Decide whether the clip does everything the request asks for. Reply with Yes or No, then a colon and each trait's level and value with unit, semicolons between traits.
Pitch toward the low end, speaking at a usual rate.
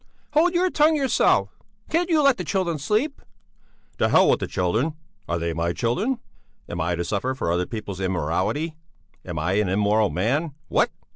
Yes: low, 115 Hz; average, 175 wpm